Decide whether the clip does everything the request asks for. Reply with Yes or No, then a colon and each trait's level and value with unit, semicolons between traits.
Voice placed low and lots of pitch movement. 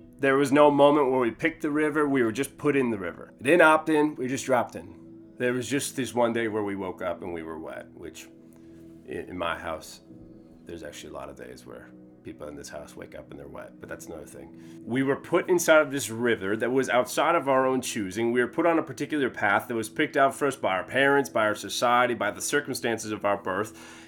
Yes: low, 120 Hz; wide, 6.9 semitones